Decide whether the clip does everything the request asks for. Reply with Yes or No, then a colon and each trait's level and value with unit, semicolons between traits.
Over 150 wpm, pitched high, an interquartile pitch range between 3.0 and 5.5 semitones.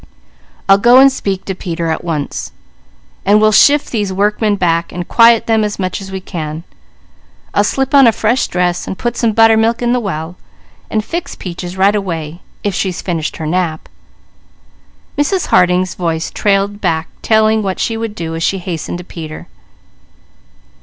Yes: average, 175 wpm; high, 195 Hz; average, 4.2 semitones